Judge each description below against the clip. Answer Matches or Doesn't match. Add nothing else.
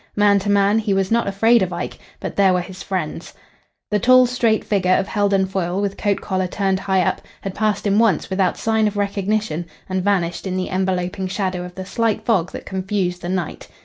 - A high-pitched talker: Matches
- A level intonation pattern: Matches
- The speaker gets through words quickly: Matches